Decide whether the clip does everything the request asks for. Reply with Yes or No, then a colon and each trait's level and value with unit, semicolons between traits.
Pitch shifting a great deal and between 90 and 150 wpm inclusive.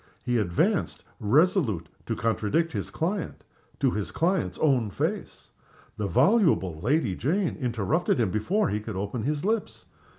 Yes: wide, 8.0 semitones; average, 140 wpm